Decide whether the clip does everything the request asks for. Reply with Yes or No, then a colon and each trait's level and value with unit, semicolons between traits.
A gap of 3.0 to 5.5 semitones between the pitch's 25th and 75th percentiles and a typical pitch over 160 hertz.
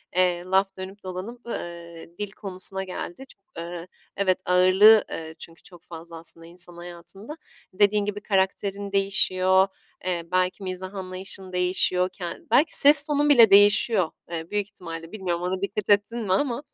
No: narrow, 2.5 semitones; medium, 185 Hz